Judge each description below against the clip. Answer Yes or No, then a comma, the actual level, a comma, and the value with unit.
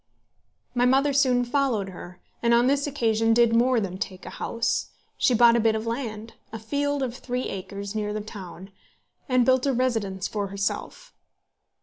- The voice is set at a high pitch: Yes, high, 230 Hz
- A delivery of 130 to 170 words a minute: No, average, 180 wpm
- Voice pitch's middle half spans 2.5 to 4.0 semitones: Yes, average, 3.5 semitones